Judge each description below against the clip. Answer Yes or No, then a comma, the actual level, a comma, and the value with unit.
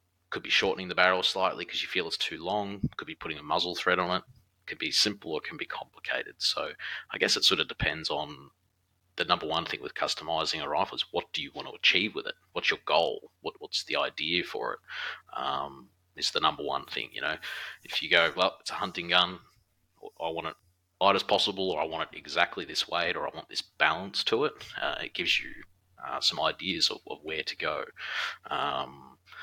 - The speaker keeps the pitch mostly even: Yes, narrow, 1.3 semitones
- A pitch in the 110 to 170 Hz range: No, very low, 90 Hz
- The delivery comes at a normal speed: No, fast, 225 wpm